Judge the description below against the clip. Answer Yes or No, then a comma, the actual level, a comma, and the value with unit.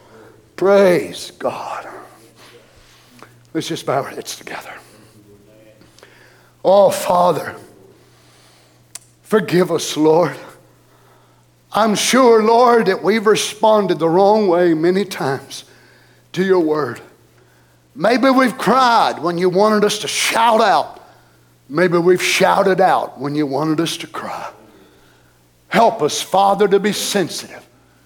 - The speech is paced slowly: Yes, slow, 115 wpm